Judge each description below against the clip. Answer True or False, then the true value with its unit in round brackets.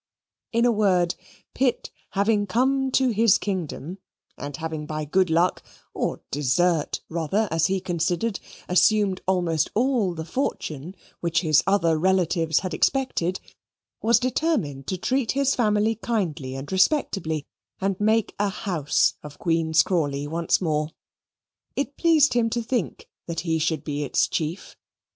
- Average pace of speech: True (145 wpm)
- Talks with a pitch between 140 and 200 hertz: True (185 Hz)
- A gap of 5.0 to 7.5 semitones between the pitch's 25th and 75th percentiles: True (5.6 semitones)